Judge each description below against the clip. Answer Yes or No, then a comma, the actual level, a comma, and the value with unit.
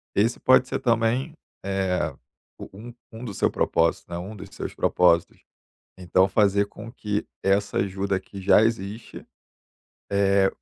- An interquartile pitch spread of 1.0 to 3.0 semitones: Yes, average, 2.7 semitones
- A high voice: No, low, 100 Hz